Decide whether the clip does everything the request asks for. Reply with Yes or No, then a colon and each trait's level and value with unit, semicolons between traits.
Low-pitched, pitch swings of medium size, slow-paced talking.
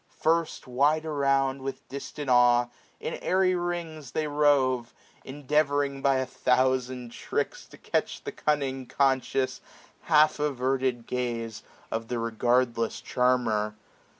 Yes: low, 130 Hz; average, 3.0 semitones; slow, 125 wpm